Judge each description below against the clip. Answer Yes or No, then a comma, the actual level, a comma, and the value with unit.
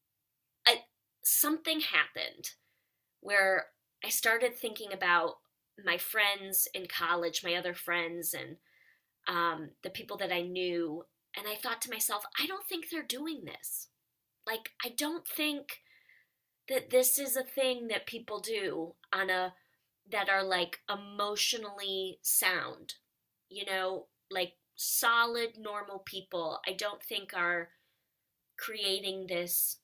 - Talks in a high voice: Yes, high, 200 Hz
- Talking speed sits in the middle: No, slow, 125 wpm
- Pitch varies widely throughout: No, average, 4.9 semitones